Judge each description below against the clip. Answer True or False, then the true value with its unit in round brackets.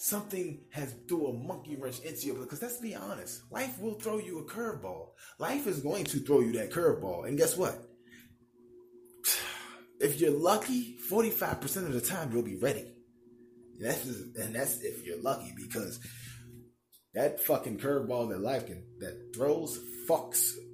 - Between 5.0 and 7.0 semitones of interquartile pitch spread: True (5.3 semitones)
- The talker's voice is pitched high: False (120 Hz)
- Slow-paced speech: False (160 wpm)